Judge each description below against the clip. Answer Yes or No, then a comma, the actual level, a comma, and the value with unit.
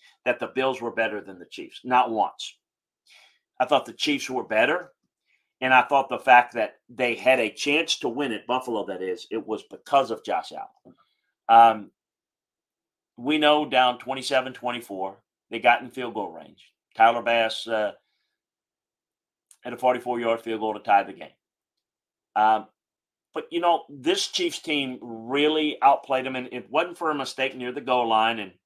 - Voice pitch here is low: Yes, low, 125 Hz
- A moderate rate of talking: Yes, average, 170 wpm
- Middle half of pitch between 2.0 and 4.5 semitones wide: Yes, average, 4.2 semitones